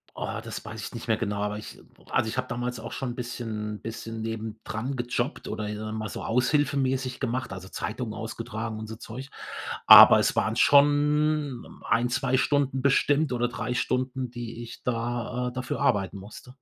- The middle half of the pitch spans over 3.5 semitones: No, average, 2.7 semitones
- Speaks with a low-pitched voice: Yes, low, 120 Hz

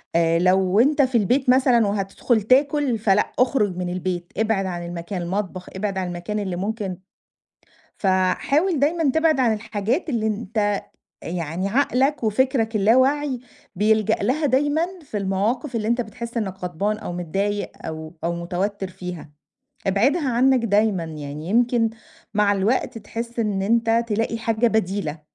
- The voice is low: No, high, 215 Hz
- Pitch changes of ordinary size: Yes, average, 4.6 semitones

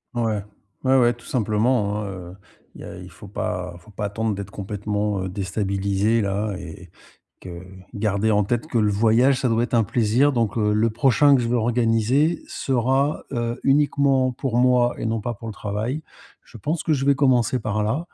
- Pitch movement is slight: No, average, 3.6 semitones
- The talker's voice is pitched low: Yes, low, 115 Hz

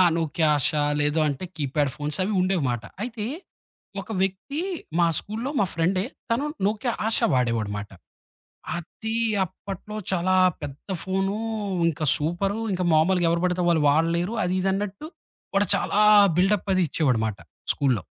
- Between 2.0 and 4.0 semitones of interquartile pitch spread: No, average, 5.0 semitones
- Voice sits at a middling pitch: Yes, medium, 180 Hz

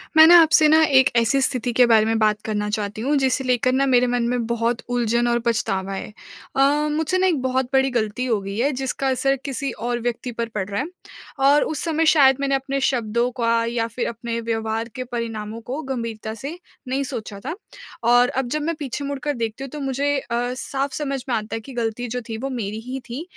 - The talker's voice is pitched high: Yes, high, 245 Hz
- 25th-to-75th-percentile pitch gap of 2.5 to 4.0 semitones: Yes, average, 3.2 semitones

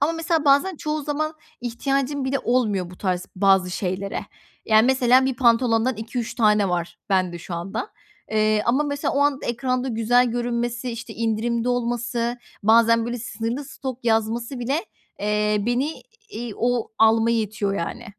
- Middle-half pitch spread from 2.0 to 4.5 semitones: Yes, average, 3.3 semitones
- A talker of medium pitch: No, high, 235 Hz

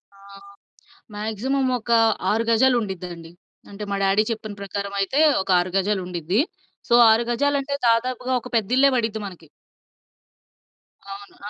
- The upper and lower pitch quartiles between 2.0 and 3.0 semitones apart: No, average, 3.7 semitones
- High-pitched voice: Yes, high, 215 Hz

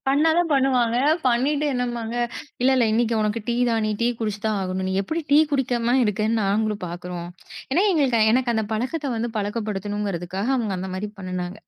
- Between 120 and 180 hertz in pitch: No, high, 225 Hz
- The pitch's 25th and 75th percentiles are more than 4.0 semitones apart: No, average, 3.7 semitones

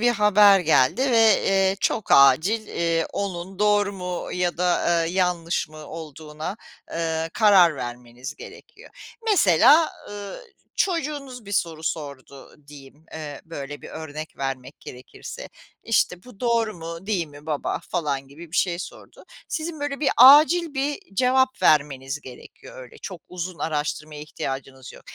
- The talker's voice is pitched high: No, medium, 175 Hz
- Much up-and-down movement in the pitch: Yes, wide, 6.3 semitones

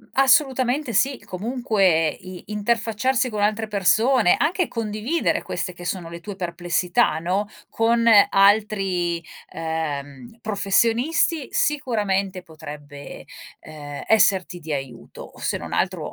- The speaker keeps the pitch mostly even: No, average, 5.3 semitones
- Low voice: No, high, 200 Hz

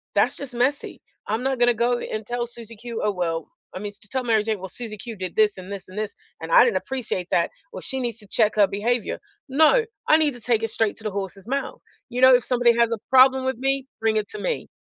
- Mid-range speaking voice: No, high, 235 Hz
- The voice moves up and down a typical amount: Yes, average, 3.8 semitones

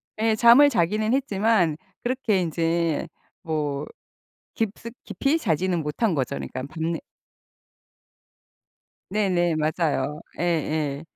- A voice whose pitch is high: No, medium, 170 Hz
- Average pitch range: No, wide, 5.8 semitones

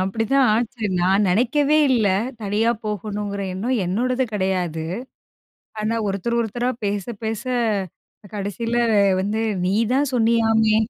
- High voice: Yes, high, 220 Hz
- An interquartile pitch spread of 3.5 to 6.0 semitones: No, average, 2.8 semitones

